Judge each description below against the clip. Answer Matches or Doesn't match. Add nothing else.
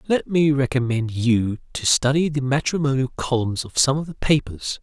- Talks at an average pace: Matches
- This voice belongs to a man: Matches